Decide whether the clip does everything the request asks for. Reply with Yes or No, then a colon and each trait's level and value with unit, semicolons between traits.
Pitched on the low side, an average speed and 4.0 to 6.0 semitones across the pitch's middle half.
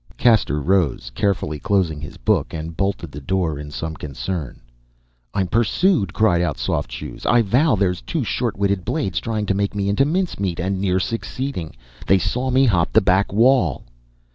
Yes: very low, 95 Hz; average, 175 wpm; average, 5.2 semitones